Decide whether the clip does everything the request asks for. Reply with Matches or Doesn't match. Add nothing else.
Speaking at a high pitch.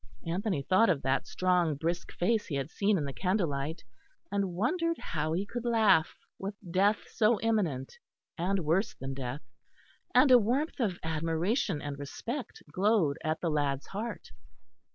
Doesn't match